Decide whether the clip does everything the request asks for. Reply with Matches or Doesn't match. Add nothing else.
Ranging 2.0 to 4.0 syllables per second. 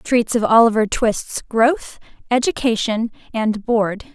Matches